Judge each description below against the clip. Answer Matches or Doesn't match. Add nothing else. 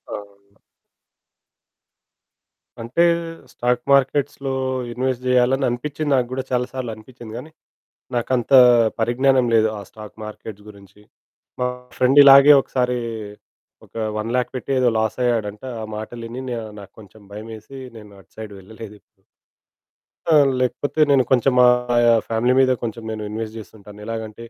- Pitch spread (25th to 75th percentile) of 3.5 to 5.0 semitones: Doesn't match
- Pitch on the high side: Doesn't match